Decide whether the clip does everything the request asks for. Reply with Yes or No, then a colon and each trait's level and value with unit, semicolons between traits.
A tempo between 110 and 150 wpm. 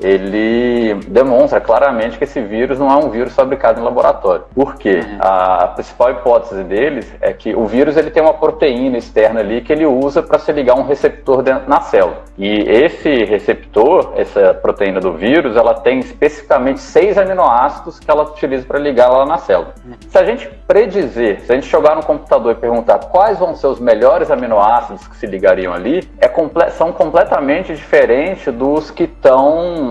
No: average, 180 wpm